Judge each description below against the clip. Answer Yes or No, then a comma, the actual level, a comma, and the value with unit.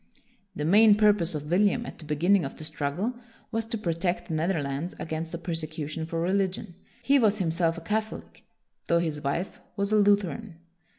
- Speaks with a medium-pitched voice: Yes, medium, 175 Hz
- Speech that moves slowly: No, average, 180 wpm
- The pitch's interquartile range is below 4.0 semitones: No, average, 4.3 semitones